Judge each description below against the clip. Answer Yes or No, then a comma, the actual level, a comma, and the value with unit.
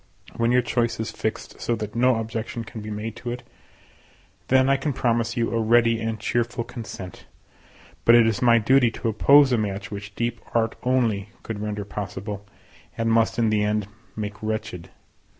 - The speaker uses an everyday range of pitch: No, narrow, 2.0 semitones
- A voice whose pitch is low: Yes, low, 115 Hz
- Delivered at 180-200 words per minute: Yes, average, 185 wpm